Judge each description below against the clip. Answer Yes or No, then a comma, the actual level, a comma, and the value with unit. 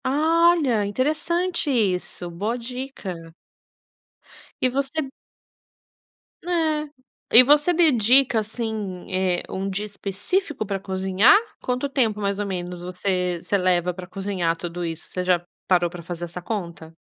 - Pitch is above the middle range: Yes, high, 205 Hz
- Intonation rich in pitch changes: Yes, wide, 6.7 semitones